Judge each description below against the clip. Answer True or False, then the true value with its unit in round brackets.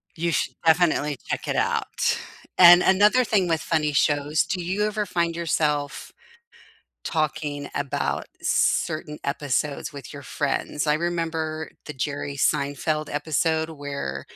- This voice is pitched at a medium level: True (155 Hz)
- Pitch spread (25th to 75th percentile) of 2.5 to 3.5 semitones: True (2.8 semitones)